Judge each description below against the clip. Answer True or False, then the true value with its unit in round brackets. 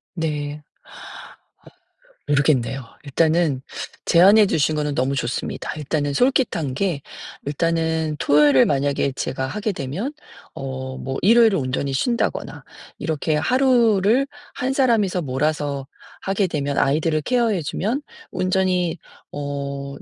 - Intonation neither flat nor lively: False (5.7 semitones)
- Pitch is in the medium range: True (155 Hz)